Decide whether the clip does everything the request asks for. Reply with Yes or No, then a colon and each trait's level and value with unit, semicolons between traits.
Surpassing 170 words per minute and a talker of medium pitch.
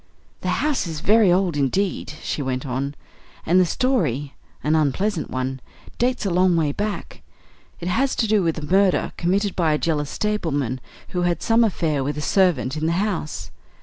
Yes: average, 180 wpm; medium, 170 Hz